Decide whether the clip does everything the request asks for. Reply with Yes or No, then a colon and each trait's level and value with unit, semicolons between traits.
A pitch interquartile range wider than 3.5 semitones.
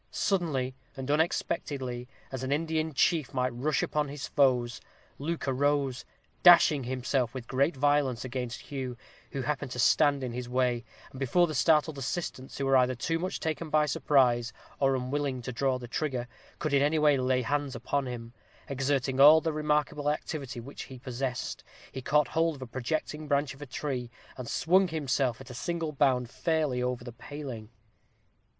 No: average, 3.0 semitones